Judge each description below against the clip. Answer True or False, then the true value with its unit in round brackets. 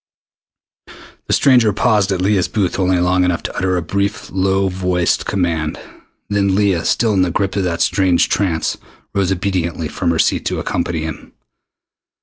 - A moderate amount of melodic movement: False (2.2 semitones)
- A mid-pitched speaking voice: False (95 Hz)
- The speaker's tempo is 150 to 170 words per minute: True (165 wpm)